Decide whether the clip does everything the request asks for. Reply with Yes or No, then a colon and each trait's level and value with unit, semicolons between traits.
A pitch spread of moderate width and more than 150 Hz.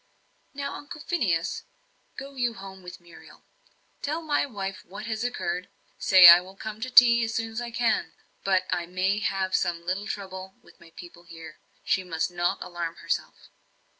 Yes: average, 4.8 semitones; high, 190 Hz